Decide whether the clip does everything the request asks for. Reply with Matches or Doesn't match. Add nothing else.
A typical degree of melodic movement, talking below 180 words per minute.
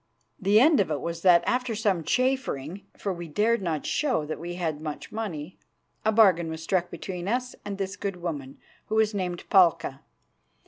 Doesn't match